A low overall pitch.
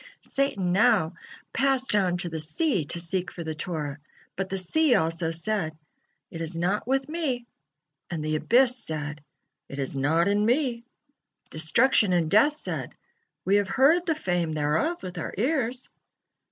No: high, 190 Hz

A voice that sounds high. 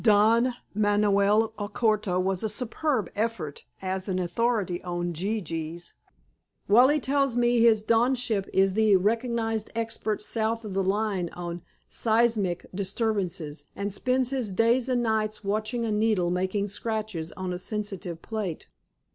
Yes: high, 210 Hz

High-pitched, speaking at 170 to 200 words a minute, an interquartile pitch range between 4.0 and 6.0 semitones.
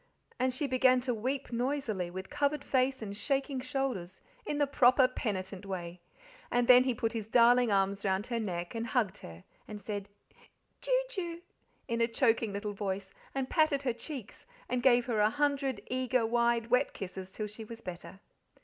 Yes: high, 235 Hz; average, 180 wpm; average, 4.4 semitones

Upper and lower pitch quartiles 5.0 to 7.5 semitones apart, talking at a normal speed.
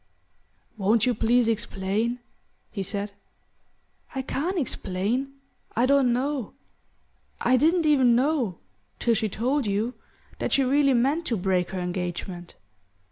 No: average, 5.3 semitones; slow, 130 wpm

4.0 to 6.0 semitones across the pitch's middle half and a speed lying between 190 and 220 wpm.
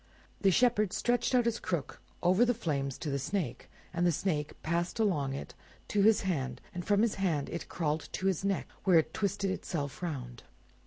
Yes: wide, 5.4 semitones; average, 200 wpm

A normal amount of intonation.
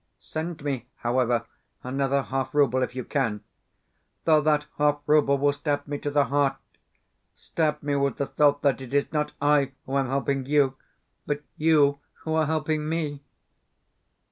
No: narrow, 1.7 semitones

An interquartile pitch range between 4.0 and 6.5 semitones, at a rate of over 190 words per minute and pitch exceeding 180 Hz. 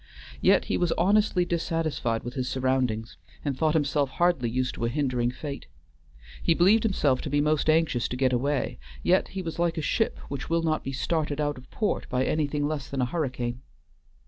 No: average, 4.4 semitones; average, 200 wpm; medium, 145 Hz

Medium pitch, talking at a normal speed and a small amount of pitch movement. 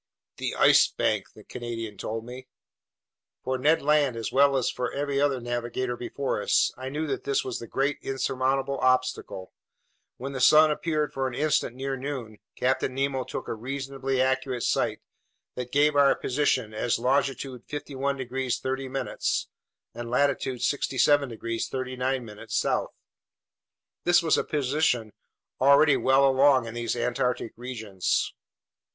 No: low, 130 Hz; average, 145 wpm; narrow, 2.2 semitones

